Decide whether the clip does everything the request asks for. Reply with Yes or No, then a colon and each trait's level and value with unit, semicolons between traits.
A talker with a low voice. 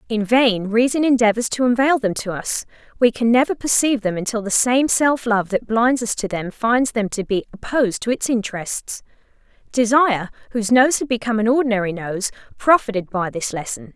No: high, 225 Hz